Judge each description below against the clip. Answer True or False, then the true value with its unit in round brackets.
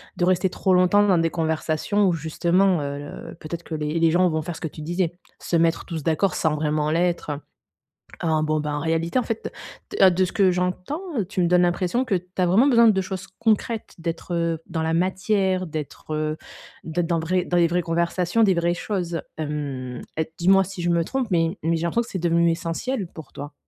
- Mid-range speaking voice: True (170 Hz)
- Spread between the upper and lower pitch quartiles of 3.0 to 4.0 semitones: False (2.5 semitones)